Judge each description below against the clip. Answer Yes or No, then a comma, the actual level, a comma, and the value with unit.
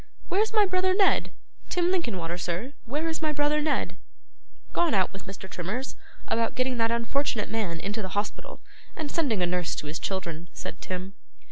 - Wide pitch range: Yes, wide, 8.7 semitones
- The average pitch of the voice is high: Yes, high, 230 Hz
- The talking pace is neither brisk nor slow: Yes, average, 180 wpm